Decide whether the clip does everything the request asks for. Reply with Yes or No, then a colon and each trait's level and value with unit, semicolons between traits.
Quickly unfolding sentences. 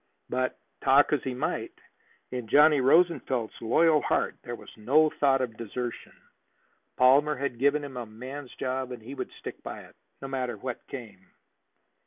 No: average, 165 wpm